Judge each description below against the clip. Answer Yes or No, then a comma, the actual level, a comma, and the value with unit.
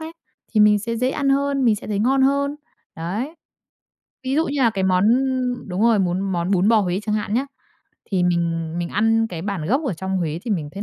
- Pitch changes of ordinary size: No, wide, 5.9 semitones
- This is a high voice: Yes, high, 210 Hz